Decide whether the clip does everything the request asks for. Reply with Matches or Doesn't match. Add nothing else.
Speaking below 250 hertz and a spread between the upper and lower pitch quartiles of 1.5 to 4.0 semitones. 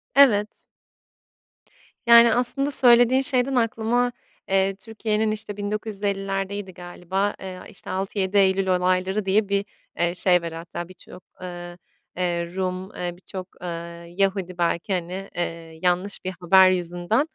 Matches